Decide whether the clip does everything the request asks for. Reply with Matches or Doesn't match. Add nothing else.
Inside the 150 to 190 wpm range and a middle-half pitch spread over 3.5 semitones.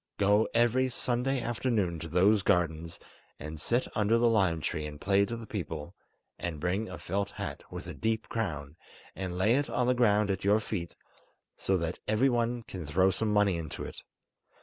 Matches